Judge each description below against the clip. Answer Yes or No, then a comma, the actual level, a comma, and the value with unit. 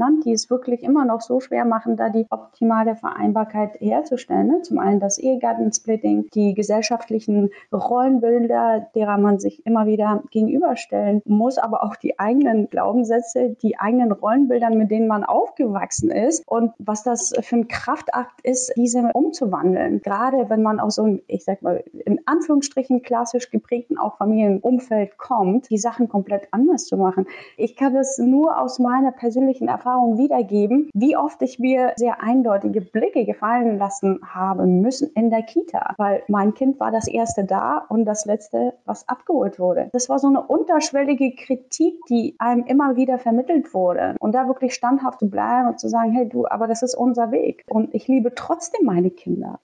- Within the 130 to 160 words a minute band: No, average, 170 wpm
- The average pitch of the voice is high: Yes, high, 235 Hz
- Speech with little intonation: No, average, 3.2 semitones